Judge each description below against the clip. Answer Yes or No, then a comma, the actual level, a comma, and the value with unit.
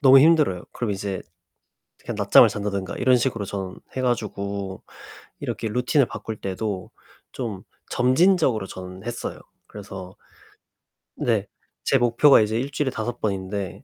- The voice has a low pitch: Yes, low, 110 Hz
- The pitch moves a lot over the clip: No, average, 4.5 semitones